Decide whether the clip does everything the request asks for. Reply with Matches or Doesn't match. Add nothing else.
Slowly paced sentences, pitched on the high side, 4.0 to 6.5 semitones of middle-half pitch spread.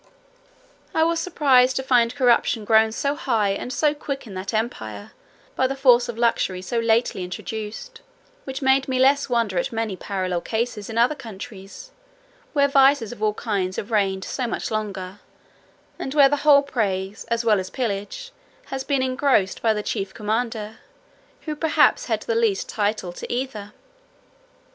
Doesn't match